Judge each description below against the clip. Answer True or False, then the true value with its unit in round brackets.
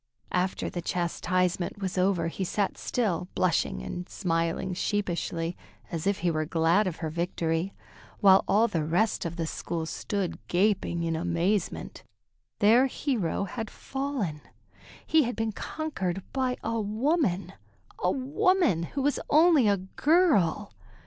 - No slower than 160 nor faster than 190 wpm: False (140 wpm)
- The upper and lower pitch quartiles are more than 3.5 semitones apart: True (5.0 semitones)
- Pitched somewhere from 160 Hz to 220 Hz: True (190 Hz)